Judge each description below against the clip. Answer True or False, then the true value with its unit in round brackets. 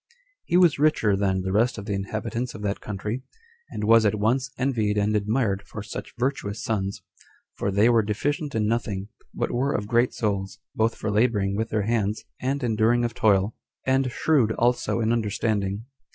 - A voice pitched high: False (110 Hz)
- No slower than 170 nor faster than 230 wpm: True (180 wpm)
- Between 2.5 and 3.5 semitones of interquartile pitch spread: True (2.9 semitones)